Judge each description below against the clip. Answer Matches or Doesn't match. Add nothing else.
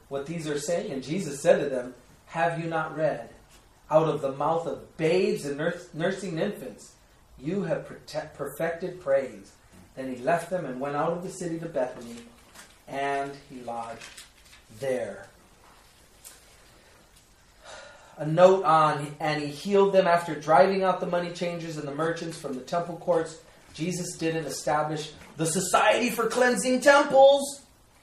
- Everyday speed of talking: Matches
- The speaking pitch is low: Doesn't match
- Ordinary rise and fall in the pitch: Matches